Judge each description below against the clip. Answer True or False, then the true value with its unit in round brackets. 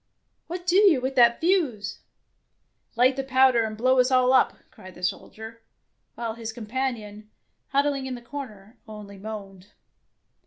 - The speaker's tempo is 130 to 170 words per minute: True (160 wpm)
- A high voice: True (240 Hz)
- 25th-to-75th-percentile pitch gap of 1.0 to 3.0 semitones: False (3.7 semitones)